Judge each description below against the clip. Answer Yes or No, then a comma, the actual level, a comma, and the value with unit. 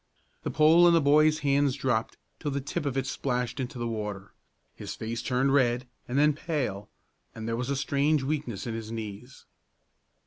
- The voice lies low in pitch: Yes, low, 130 Hz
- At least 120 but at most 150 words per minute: No, average, 185 wpm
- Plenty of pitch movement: No, average, 3.8 semitones